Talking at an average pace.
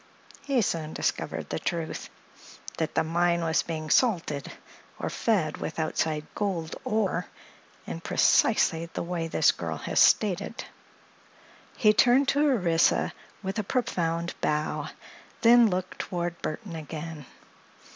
No: slow, 125 wpm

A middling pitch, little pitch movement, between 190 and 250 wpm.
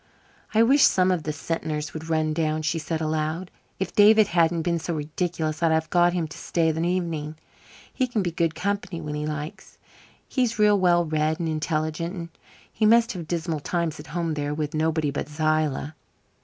Yes: medium, 160 Hz; narrow, 2.3 semitones; average, 195 wpm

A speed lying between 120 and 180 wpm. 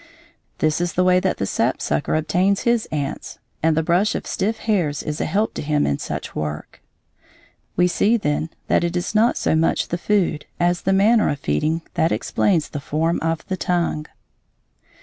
No: average, 190 wpm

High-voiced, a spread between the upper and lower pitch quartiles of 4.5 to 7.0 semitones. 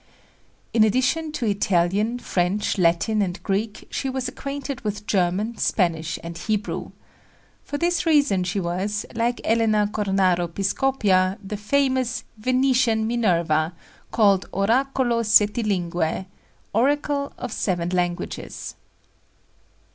Yes: high, 210 Hz; average, 5.1 semitones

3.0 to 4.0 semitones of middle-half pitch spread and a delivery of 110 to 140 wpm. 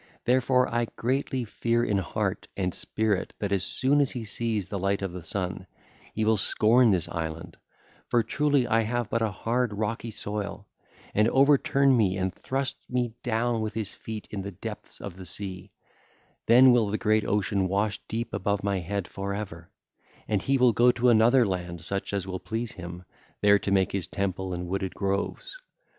No: average, 3.7 semitones; average, 180 wpm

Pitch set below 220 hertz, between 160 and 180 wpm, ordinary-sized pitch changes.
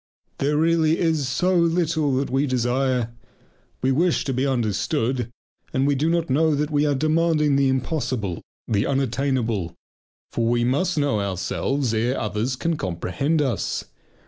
No: low, 135 Hz; average, 150 wpm; average, 4.2 semitones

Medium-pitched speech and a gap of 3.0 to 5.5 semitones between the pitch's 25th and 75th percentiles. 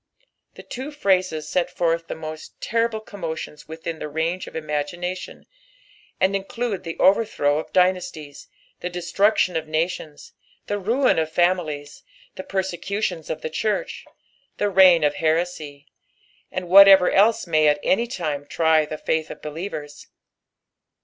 Yes: medium, 175 Hz; average, 3.6 semitones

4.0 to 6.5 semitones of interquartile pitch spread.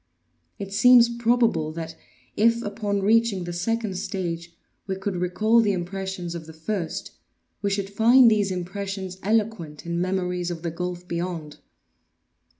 No: average, 3.6 semitones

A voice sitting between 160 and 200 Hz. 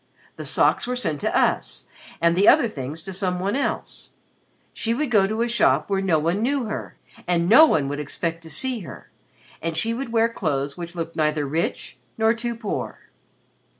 Yes: high, 190 Hz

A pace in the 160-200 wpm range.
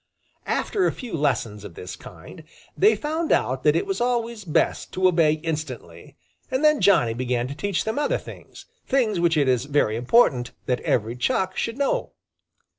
Yes: average, 180 wpm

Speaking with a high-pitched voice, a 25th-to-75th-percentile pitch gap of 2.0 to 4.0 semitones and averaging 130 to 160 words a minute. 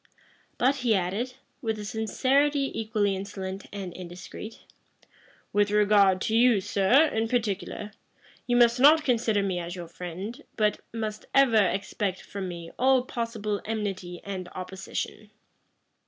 Yes: high, 210 Hz; average, 3.7 semitones; slow, 135 wpm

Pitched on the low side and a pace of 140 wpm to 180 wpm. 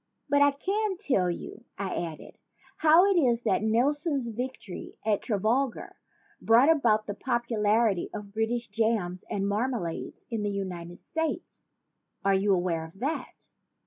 No: high, 225 Hz; average, 145 wpm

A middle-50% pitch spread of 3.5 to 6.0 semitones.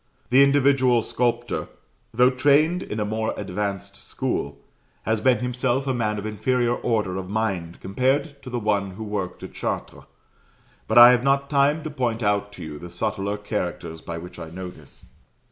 Yes: average, 4.4 semitones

